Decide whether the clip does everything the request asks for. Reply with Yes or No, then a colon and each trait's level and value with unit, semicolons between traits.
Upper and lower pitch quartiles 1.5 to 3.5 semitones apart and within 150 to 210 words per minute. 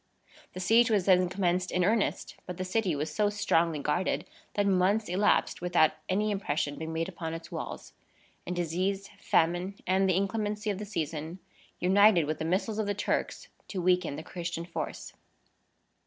Yes: average, 3.2 semitones; average, 170 wpm